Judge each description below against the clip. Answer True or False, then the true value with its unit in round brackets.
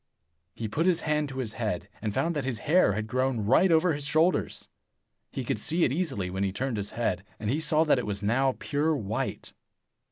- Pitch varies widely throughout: True (6.6 semitones)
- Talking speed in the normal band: False (220 wpm)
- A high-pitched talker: False (130 Hz)